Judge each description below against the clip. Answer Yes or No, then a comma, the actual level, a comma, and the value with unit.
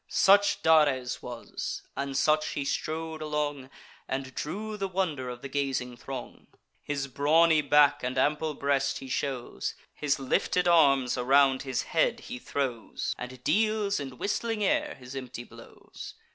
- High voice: No, medium, 140 Hz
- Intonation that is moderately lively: Yes, average, 3.7 semitones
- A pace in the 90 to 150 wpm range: Yes, average, 145 wpm